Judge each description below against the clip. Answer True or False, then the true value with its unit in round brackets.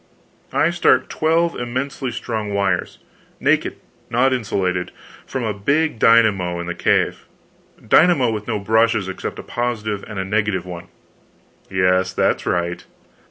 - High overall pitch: False (110 Hz)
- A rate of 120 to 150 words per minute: True (140 wpm)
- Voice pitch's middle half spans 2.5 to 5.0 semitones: True (4.7 semitones)